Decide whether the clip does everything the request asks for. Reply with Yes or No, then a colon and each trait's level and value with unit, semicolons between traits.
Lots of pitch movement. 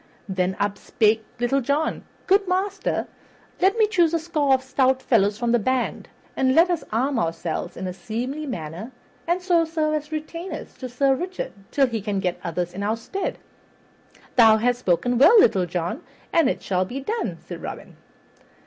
Yes: wide, 7.7 semitones